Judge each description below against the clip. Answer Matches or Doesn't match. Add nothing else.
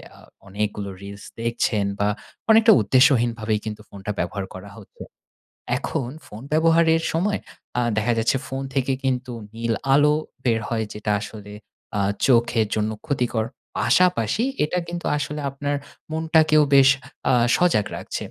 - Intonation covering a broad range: Matches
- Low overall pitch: Matches